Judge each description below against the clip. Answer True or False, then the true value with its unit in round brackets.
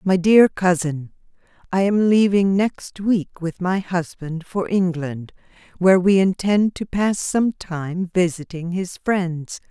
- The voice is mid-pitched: True (180 Hz)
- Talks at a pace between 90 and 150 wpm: True (140 wpm)